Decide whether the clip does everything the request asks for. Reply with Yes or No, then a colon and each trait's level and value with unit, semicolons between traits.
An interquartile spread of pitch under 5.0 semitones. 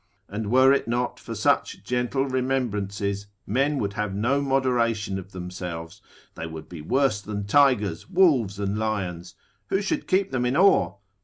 No: average, 5.3 semitones